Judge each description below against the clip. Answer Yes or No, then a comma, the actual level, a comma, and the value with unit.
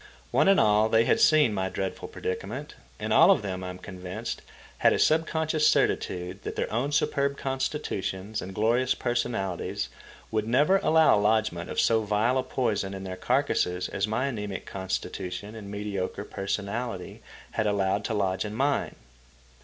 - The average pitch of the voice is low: Yes, low, 105 Hz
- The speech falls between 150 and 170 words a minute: Yes, average, 160 wpm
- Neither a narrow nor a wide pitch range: Yes, average, 5.0 semitones